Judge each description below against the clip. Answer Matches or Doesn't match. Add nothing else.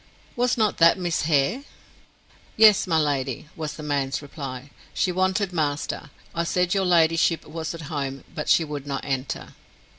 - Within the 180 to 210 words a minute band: Doesn't match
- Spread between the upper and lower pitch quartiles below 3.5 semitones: Doesn't match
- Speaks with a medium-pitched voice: Matches